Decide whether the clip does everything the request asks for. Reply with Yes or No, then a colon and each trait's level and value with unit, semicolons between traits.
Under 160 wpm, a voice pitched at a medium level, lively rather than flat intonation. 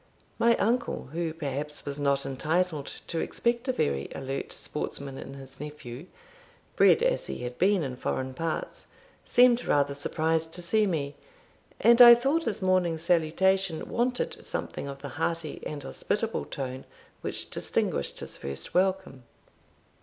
Yes: average, 145 wpm; medium, 160 Hz; wide, 5.8 semitones